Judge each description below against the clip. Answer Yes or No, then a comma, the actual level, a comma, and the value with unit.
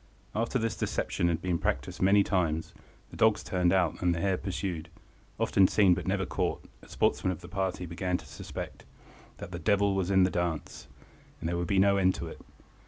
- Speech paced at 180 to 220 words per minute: Yes, average, 200 wpm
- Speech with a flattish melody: Yes, narrow, 2.0 semitones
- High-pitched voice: No, very low, 95 Hz